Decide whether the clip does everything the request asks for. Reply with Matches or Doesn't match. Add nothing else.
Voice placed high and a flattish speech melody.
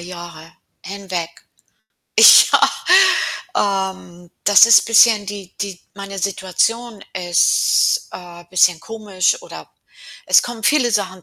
Doesn't match